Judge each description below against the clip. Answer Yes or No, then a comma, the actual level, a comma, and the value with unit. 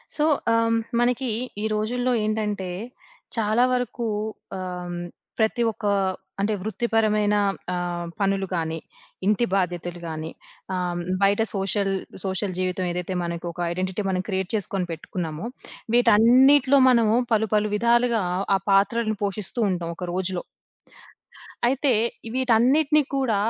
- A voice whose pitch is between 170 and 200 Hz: No, high, 210 Hz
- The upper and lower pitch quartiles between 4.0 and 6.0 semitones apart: Yes, average, 4.3 semitones